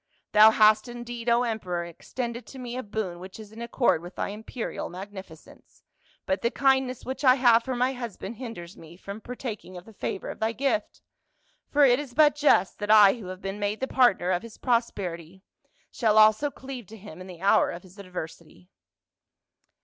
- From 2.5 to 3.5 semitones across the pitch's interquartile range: No, average, 4.6 semitones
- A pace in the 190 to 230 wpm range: Yes, average, 195 wpm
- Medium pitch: No, high, 220 Hz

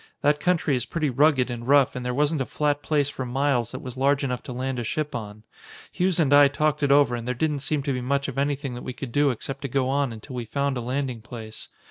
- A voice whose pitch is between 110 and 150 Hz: Yes, low, 135 Hz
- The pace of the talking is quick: Yes, fast, 265 wpm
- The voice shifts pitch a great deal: No, narrow, 2.6 semitones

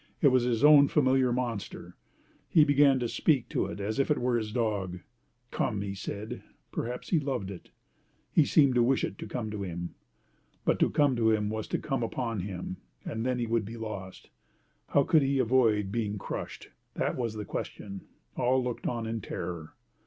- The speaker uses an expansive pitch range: No, average, 4.0 semitones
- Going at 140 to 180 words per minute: No, average, 195 wpm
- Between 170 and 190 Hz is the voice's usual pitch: No, low, 115 Hz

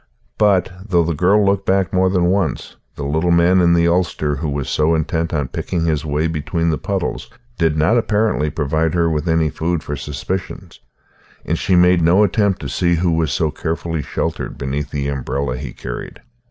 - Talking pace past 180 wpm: Yes, average, 195 wpm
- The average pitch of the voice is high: No, very low, 80 Hz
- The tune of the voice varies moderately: Yes, average, 3.0 semitones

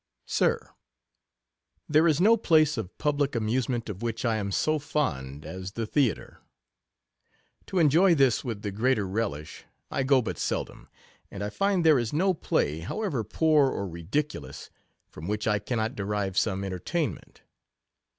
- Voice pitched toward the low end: Yes, low, 115 Hz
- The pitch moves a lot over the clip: Yes, wide, 7.1 semitones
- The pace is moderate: Yes, average, 160 wpm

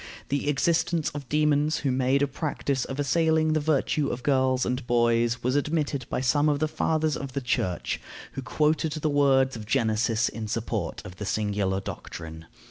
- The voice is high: No, low, 135 Hz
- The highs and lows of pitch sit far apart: No, average, 4.2 semitones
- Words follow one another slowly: No, average, 180 wpm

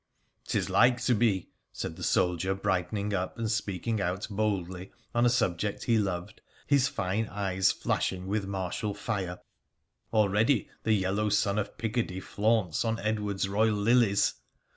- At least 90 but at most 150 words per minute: No, average, 165 wpm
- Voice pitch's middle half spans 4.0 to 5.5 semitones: No, average, 2.8 semitones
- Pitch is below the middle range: Yes, low, 105 Hz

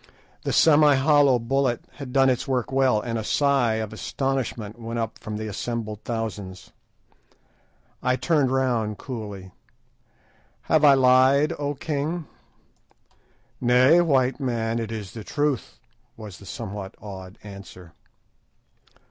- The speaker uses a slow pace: Yes, slow, 130 wpm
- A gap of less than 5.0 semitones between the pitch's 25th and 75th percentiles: Yes, average, 4.0 semitones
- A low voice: Yes, low, 120 Hz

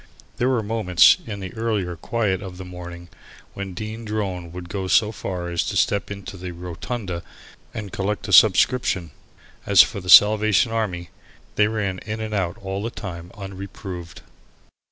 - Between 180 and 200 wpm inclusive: No, average, 170 wpm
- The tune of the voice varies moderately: Yes, average, 3.2 semitones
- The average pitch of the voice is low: Yes, very low, 95 Hz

